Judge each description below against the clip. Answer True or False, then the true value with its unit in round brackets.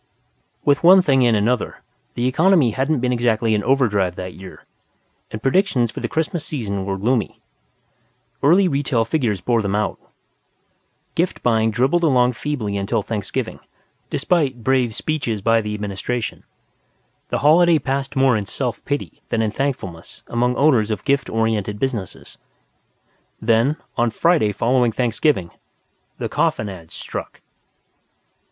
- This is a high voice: False (120 Hz)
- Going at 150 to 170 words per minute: False (140 wpm)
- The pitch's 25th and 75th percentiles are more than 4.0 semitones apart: True (4.5 semitones)